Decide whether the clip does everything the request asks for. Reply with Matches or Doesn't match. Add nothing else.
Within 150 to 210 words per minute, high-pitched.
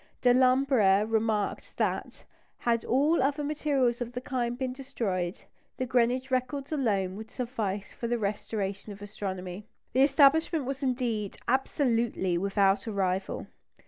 Doesn't match